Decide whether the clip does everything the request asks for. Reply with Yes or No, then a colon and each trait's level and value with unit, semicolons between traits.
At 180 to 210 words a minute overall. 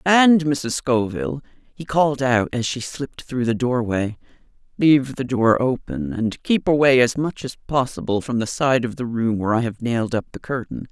Yes: average, 200 wpm